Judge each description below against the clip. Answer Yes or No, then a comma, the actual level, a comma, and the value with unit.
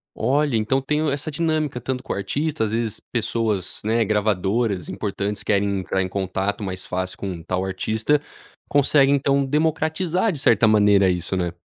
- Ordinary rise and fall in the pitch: No, wide, 6.2 semitones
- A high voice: No, low, 110 Hz